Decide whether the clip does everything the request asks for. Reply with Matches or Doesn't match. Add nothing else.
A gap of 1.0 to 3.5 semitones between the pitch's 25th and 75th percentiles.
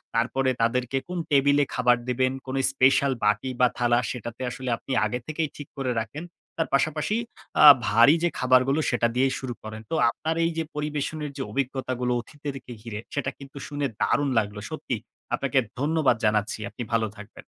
Matches